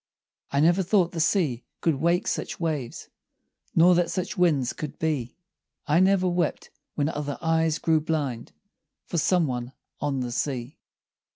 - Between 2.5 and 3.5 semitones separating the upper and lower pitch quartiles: No, average, 3.9 semitones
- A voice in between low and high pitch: Yes, medium, 160 Hz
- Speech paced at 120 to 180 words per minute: Yes, average, 155 wpm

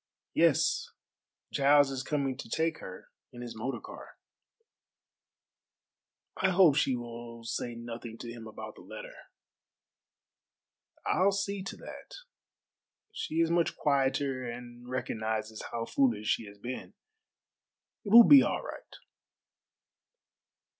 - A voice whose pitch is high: No, low, 130 Hz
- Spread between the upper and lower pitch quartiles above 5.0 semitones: Yes, wide, 5.5 semitones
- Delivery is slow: Yes, slow, 120 wpm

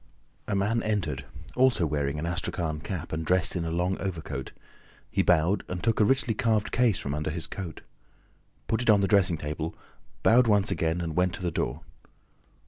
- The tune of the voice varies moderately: Yes, average, 4.5 semitones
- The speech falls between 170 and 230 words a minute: Yes, average, 190 wpm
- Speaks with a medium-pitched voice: No, very low, 90 Hz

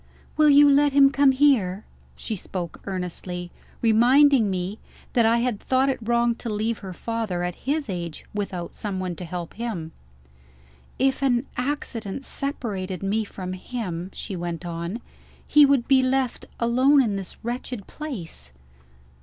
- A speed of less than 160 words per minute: Yes, average, 150 wpm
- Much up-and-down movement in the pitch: Yes, wide, 6.2 semitones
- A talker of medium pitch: No, high, 225 Hz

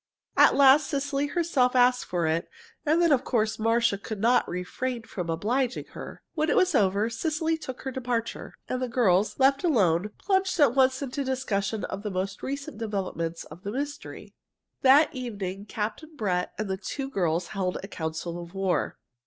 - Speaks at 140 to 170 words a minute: No, average, 180 wpm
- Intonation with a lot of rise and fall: Yes, wide, 6.0 semitones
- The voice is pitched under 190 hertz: No, high, 230 Hz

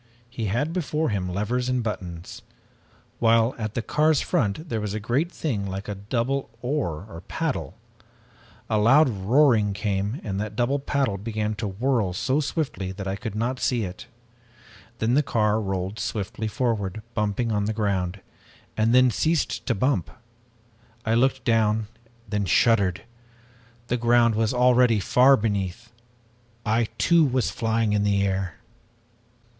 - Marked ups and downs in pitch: No, average, 3.9 semitones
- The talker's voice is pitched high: No, low, 110 Hz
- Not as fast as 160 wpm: Yes, average, 150 wpm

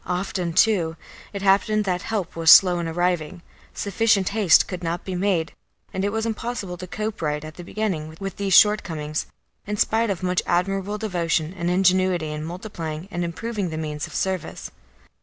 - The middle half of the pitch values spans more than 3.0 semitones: Yes, average, 3.4 semitones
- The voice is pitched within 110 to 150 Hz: No, medium, 180 Hz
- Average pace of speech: Yes, average, 175 wpm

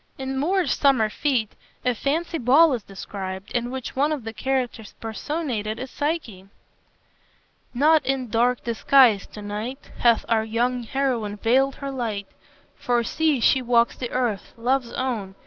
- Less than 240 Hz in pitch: No, high, 245 Hz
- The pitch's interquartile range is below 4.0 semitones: Yes, average, 3.4 semitones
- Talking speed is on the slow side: No, average, 155 wpm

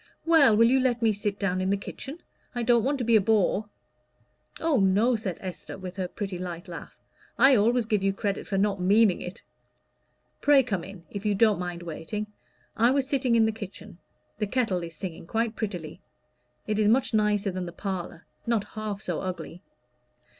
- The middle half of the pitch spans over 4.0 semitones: No, average, 3.6 semitones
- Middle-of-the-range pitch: No, high, 205 Hz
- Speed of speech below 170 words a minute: No, average, 195 wpm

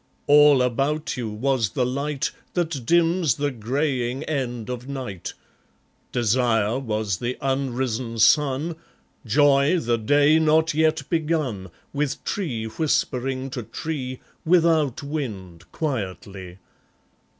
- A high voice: No, low, 135 Hz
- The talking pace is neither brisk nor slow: No, slow, 110 wpm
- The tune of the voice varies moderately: Yes, average, 4.3 semitones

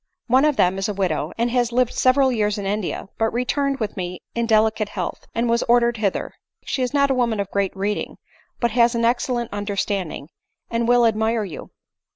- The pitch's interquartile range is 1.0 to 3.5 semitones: Yes, average, 3.1 semitones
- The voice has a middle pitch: No, high, 230 Hz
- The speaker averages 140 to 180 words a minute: No, average, 200 wpm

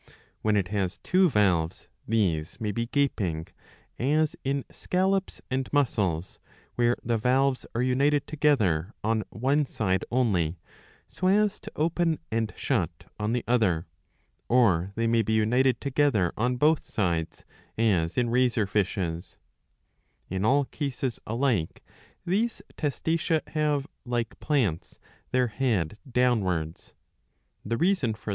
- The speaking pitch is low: Yes, low, 120 Hz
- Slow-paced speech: Yes, slow, 130 wpm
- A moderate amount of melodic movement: No, wide, 6.0 semitones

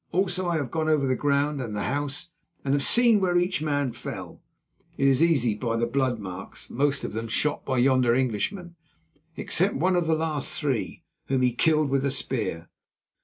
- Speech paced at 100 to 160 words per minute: No, average, 185 wpm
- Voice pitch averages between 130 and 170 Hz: Yes, medium, 140 Hz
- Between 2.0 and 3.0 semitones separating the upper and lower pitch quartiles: No, average, 4.1 semitones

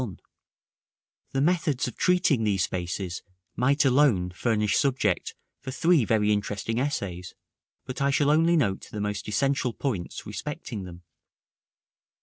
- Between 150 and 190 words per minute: No, slow, 135 wpm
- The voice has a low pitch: Yes, low, 115 Hz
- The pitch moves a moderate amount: No, wide, 5.9 semitones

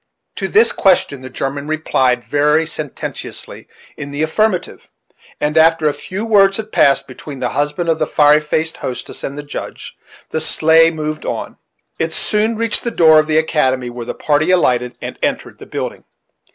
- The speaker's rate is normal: Yes, average, 180 wpm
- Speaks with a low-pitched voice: No, medium, 155 Hz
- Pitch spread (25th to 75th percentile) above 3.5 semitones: No, average, 2.7 semitones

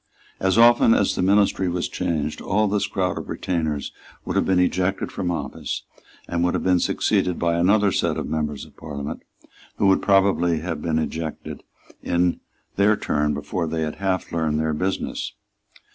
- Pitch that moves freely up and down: No, average, 3.4 semitones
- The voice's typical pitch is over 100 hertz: No, very low, 90 Hz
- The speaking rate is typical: Yes, average, 175 wpm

